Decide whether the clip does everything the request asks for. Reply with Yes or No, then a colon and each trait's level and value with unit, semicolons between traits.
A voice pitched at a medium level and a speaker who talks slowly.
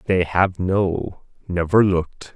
No: very low, 90 Hz; slow, 130 wpm